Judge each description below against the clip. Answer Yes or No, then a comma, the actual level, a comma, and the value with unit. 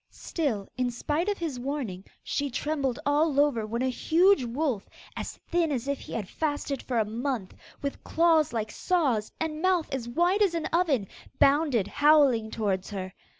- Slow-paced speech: No, average, 175 wpm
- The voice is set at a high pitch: Yes, very high, 280 Hz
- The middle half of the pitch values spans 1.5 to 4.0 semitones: No, wide, 5.5 semitones